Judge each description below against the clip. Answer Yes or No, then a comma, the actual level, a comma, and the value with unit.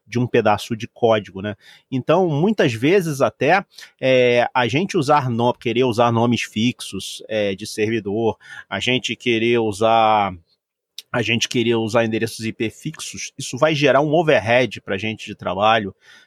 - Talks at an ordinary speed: Yes, average, 160 wpm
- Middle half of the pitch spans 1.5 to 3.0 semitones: Yes, narrow, 2.5 semitones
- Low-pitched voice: Yes, low, 115 Hz